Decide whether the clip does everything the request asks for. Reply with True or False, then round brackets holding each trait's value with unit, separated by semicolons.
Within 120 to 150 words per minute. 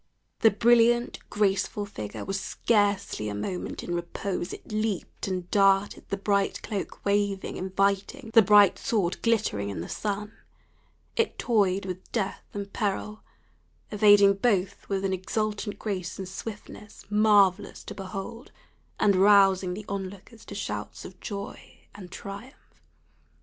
True (140 wpm)